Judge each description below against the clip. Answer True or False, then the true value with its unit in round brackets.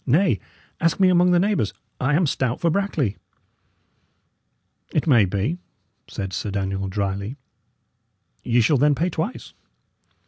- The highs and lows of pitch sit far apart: True (9.0 semitones)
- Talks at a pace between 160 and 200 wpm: False (135 wpm)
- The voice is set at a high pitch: False (135 Hz)